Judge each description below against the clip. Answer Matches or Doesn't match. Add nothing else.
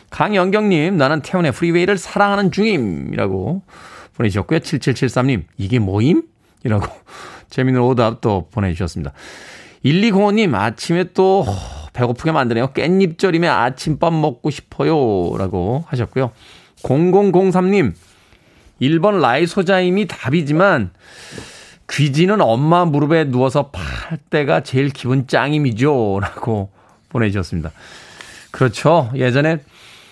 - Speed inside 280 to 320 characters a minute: Doesn't match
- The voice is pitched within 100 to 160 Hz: Matches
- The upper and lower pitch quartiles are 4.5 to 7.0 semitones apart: Doesn't match